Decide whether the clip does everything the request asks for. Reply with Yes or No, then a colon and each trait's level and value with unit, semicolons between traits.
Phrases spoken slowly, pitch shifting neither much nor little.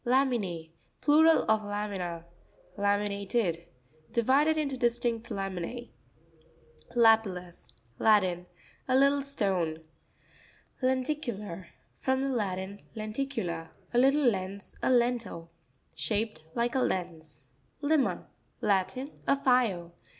No: slow, 85 wpm; wide, 6.1 semitones